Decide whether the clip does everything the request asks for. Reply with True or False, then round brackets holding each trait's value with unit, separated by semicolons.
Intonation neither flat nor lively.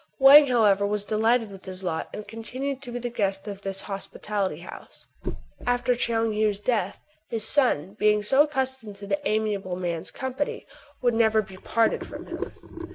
True (3.7 semitones)